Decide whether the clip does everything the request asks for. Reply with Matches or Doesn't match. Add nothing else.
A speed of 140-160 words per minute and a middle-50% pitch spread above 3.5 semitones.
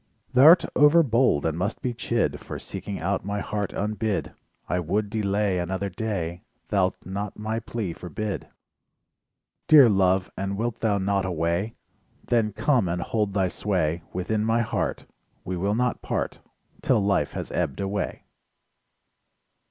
Doesn't match